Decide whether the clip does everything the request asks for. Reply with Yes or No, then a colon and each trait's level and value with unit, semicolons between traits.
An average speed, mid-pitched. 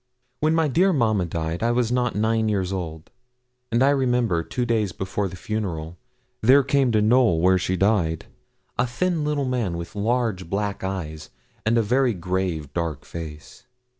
No: average, 170 wpm; low, 105 Hz